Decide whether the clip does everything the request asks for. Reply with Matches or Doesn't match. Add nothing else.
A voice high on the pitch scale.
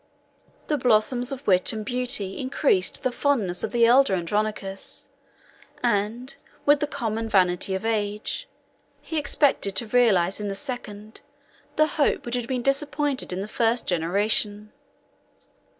Matches